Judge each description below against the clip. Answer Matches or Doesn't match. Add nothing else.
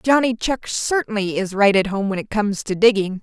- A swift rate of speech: Matches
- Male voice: Doesn't match